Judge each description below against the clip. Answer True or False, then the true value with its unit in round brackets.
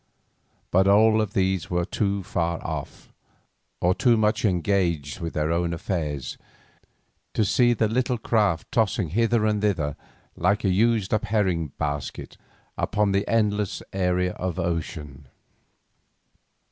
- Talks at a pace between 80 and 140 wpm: True (135 wpm)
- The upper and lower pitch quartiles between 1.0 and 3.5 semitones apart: False (4.0 semitones)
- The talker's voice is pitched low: True (95 Hz)